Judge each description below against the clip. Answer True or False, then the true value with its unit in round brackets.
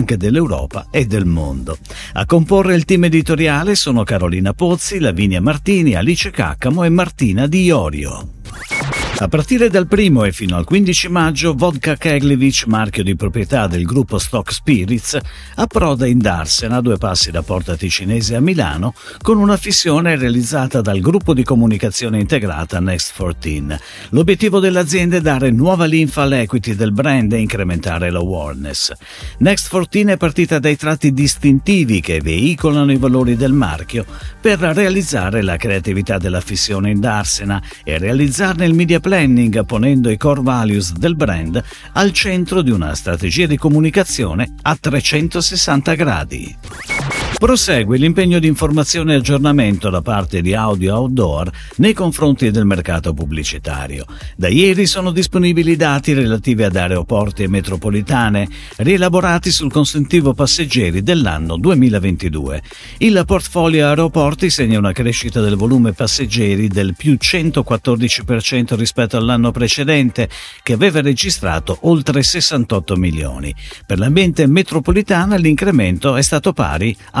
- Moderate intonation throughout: False (8.4 semitones)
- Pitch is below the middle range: True (125 Hz)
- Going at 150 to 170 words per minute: False (135 wpm)